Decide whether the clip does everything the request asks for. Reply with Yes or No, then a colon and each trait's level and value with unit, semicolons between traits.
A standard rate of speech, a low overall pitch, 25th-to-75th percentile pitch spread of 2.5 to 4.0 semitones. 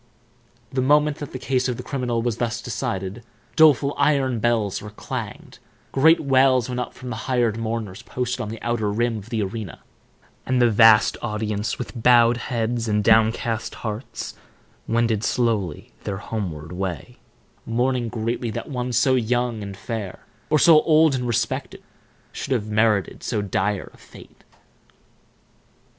Yes: average, 155 wpm; low, 115 Hz; average, 2.8 semitones